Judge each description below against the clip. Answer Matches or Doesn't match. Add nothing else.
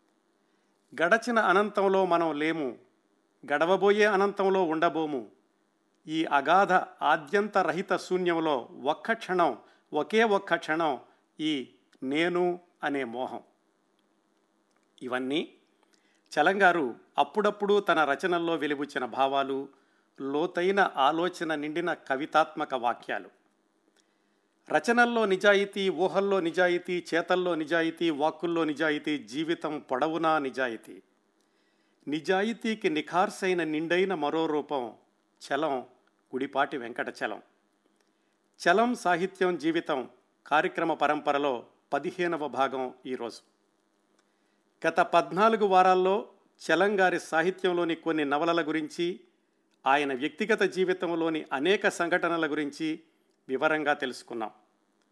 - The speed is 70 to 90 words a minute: Matches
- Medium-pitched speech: Matches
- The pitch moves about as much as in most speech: Matches